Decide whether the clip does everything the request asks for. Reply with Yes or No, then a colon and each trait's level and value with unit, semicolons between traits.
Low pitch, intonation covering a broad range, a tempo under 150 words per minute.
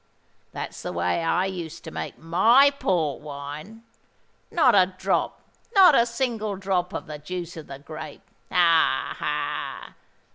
No: medium, 180 Hz; wide, 5.8 semitones; average, 140 wpm